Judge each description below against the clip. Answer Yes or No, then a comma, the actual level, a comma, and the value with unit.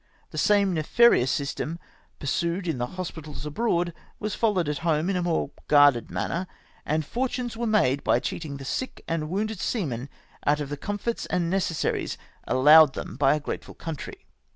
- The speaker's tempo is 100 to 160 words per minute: No, average, 170 wpm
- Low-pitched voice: No, medium, 165 Hz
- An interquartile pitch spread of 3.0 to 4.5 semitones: No, average, 5.2 semitones